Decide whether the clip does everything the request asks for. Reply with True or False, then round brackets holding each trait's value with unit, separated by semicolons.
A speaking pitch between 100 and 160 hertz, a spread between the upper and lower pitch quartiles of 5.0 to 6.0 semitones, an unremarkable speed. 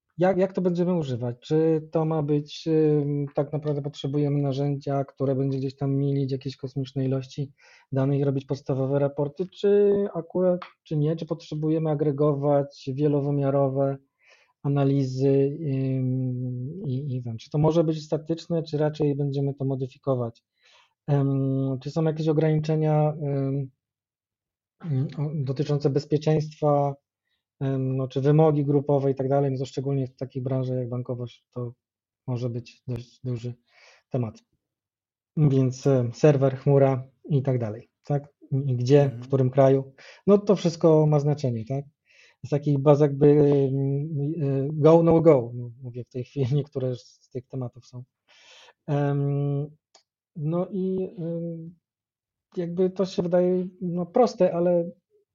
False (140 Hz; 2.7 semitones; 125 wpm)